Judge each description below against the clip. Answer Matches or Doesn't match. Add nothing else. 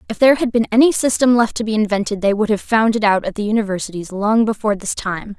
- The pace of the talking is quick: Matches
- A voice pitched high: Matches